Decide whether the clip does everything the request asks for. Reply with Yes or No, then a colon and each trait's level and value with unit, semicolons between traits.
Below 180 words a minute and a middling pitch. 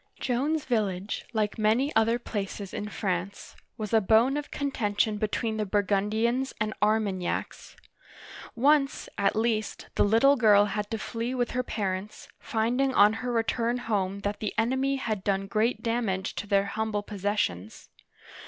No: average, 155 wpm; high, 220 Hz